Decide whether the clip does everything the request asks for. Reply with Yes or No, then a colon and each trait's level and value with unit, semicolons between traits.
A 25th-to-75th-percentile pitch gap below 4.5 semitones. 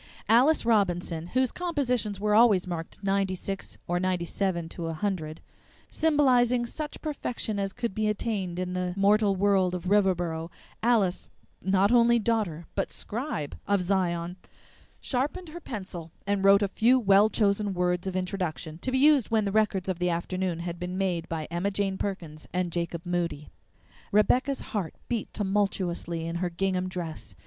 Yes: average, 3.6 semitones